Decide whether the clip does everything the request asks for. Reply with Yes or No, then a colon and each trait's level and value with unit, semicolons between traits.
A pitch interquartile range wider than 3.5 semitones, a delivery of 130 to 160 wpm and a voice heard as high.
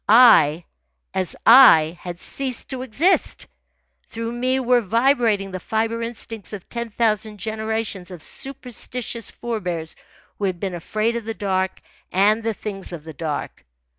Yes: average, 3.9 semitones; average, 145 wpm; high, 220 Hz